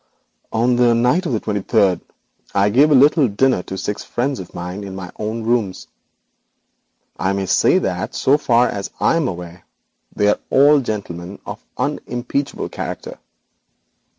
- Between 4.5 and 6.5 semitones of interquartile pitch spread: Yes, average, 4.9 semitones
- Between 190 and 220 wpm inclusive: No, average, 160 wpm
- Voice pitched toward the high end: No, low, 110 Hz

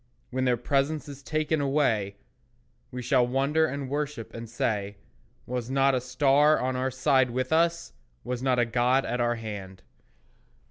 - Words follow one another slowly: No, average, 165 wpm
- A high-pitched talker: No, low, 130 Hz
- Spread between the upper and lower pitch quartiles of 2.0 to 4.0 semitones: Yes, average, 2.8 semitones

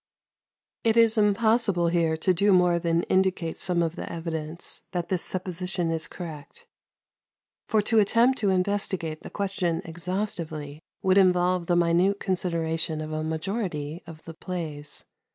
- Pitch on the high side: No, medium, 175 Hz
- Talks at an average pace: Yes, average, 150 wpm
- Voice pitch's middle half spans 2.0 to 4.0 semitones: Yes, average, 2.9 semitones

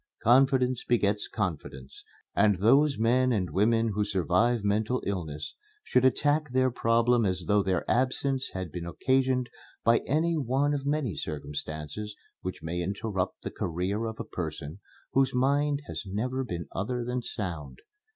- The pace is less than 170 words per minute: Yes, average, 150 wpm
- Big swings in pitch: Yes, wide, 5.7 semitones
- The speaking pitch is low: Yes, low, 115 Hz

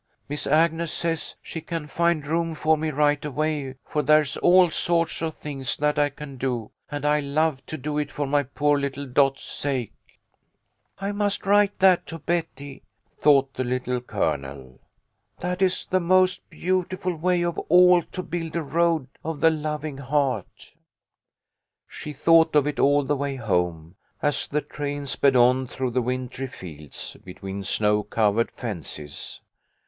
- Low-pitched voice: No, medium, 145 Hz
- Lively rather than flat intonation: No, average, 4.0 semitones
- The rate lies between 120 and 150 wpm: No, average, 165 wpm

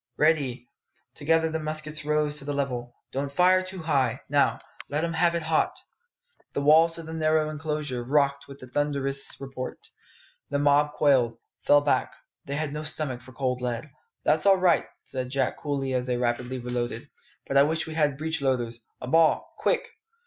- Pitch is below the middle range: No, medium, 145 Hz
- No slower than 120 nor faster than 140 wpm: No, average, 180 wpm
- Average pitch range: Yes, average, 3.2 semitones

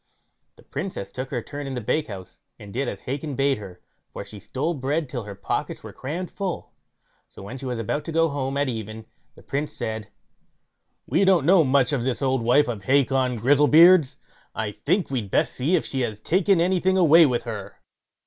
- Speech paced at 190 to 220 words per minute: Yes, average, 200 wpm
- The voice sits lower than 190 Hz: Yes, low, 135 Hz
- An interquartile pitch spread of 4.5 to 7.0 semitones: Yes, average, 5.1 semitones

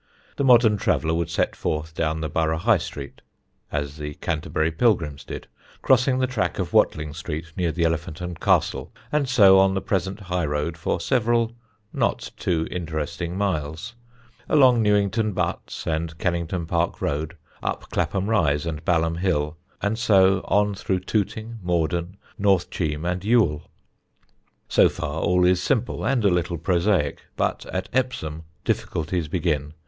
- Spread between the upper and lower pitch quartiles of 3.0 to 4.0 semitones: No, average, 4.4 semitones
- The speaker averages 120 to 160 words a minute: Yes, average, 155 wpm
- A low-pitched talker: Yes, very low, 85 Hz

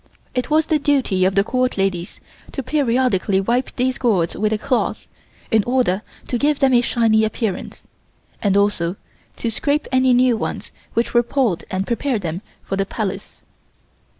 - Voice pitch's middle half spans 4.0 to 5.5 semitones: Yes, average, 4.7 semitones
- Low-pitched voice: No, high, 230 Hz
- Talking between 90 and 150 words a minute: No, average, 170 wpm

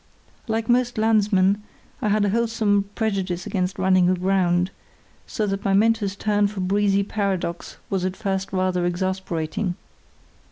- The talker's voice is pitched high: Yes, high, 195 Hz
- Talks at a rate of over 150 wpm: No, slow, 135 wpm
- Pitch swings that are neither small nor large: No, narrow, 2.1 semitones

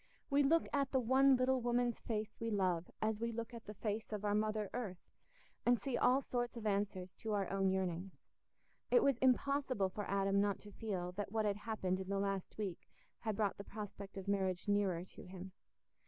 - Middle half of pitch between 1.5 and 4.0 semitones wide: Yes, average, 3.5 semitones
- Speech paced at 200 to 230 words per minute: Yes, fast, 205 wpm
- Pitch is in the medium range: No, high, 210 Hz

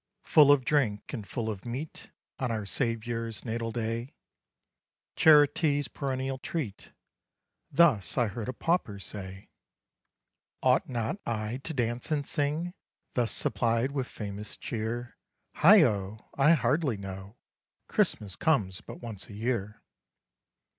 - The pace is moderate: No, slow, 125 wpm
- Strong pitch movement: No, average, 4.7 semitones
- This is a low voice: Yes, low, 120 Hz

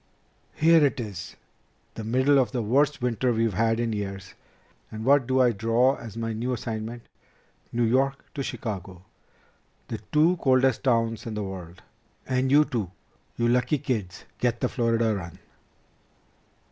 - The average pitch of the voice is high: No, low, 120 Hz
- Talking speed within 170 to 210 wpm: No, average, 155 wpm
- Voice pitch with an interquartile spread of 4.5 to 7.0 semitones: No, average, 3.2 semitones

